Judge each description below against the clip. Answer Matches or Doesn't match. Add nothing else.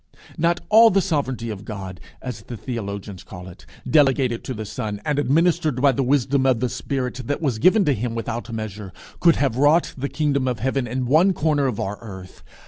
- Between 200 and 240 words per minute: Matches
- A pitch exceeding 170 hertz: Doesn't match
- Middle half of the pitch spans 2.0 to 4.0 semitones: Doesn't match